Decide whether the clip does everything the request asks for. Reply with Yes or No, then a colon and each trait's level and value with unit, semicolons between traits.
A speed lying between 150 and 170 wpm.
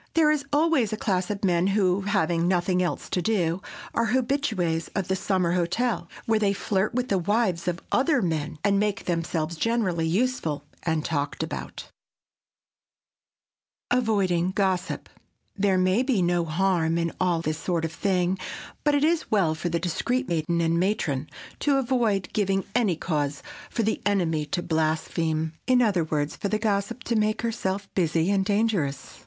Yes: average, 165 wpm